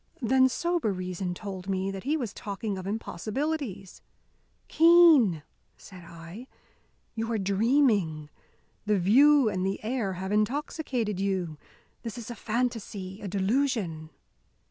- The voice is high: Yes, high, 210 Hz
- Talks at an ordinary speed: No, slow, 125 wpm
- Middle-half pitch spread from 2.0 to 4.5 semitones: No, average, 5.0 semitones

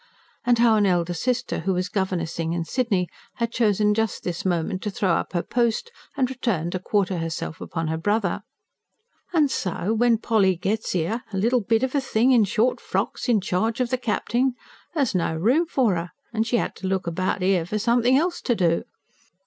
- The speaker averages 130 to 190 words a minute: No, fast, 205 wpm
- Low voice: No, high, 210 Hz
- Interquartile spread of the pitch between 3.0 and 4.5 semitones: No, average, 5.0 semitones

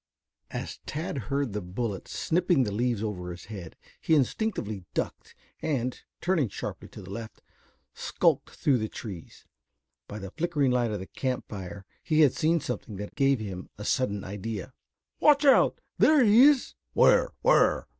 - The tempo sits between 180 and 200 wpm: No, average, 165 wpm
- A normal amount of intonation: No, wide, 7.4 semitones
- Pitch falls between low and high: No, low, 120 Hz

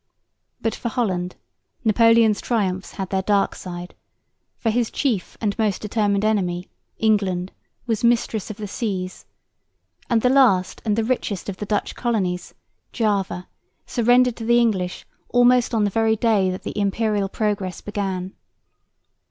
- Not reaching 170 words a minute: Yes, average, 145 wpm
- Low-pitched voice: No, high, 210 Hz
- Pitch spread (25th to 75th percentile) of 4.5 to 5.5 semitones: No, average, 3.2 semitones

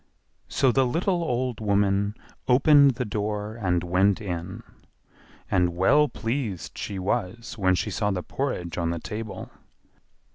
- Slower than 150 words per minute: Yes, average, 140 wpm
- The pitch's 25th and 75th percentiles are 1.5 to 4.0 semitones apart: No, average, 4.9 semitones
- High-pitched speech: No, low, 105 Hz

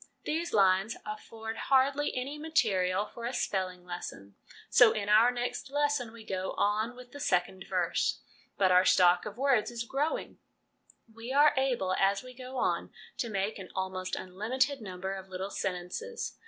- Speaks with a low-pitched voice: No, high, 220 Hz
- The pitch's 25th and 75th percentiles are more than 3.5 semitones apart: Yes, wide, 5.5 semitones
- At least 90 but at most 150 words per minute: No, average, 165 wpm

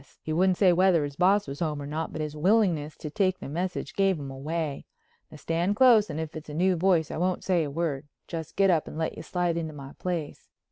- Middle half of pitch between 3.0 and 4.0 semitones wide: Yes, average, 3.5 semitones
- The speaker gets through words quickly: Yes, fast, 245 wpm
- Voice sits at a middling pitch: Yes, medium, 165 Hz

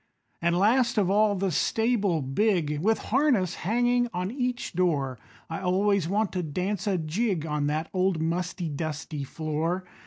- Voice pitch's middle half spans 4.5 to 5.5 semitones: Yes, average, 4.8 semitones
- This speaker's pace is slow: No, average, 155 wpm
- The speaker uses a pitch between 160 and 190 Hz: Yes, medium, 185 Hz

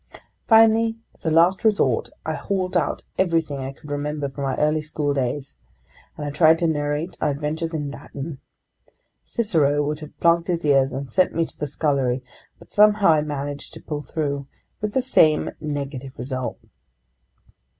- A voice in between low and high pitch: Yes, medium, 150 Hz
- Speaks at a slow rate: No, average, 165 wpm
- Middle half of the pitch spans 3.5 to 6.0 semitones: No, average, 2.9 semitones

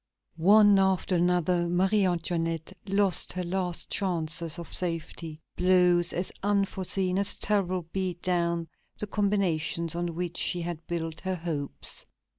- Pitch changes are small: Yes, narrow, 2.1 semitones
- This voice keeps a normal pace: No, slow, 130 wpm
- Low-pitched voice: No, medium, 180 Hz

